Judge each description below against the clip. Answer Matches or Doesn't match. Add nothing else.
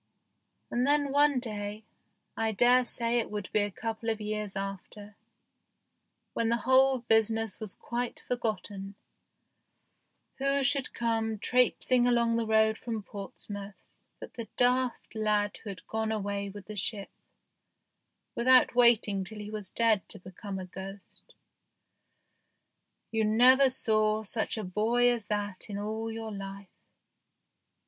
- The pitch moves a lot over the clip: Doesn't match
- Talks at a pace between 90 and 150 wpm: Matches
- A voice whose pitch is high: Matches